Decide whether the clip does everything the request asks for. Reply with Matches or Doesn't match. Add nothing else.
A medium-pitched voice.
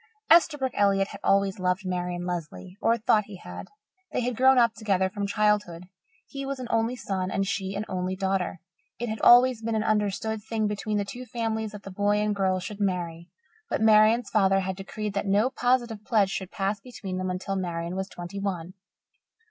Doesn't match